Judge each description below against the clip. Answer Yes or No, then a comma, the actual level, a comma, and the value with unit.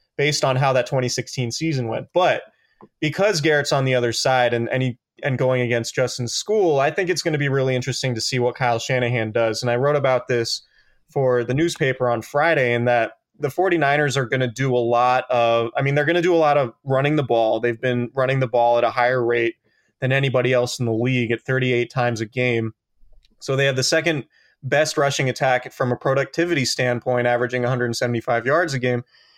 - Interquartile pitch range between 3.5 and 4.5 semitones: No, narrow, 2.5 semitones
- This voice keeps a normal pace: No, fast, 215 wpm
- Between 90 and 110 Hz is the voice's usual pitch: No, low, 125 Hz